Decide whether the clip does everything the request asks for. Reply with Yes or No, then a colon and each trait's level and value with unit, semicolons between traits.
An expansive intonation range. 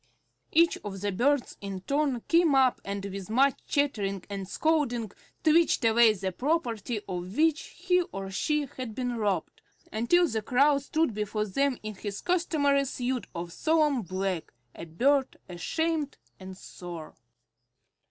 Yes: wide, 6.7 semitones